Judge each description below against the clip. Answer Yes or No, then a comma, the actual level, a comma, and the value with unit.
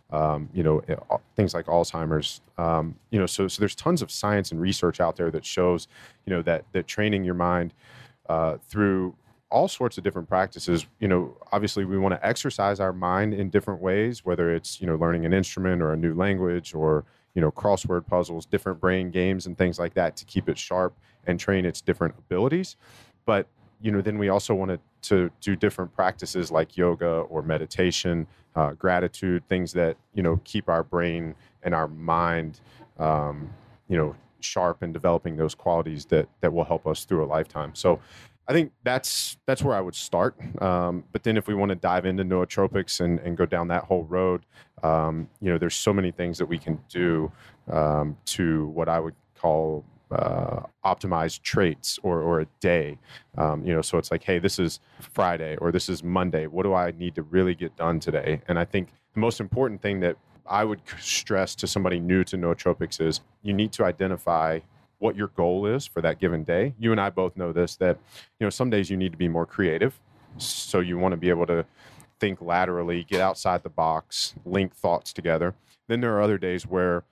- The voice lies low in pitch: Yes, very low, 90 Hz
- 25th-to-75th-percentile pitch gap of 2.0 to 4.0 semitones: Yes, average, 3.1 semitones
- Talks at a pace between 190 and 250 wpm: Yes, fast, 205 wpm